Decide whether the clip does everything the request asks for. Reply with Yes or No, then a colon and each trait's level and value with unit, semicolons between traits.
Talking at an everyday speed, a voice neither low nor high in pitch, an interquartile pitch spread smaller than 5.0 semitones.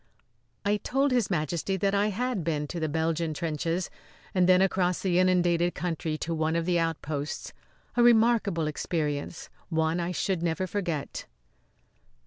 Yes: average, 150 wpm; medium, 175 Hz; average, 3.1 semitones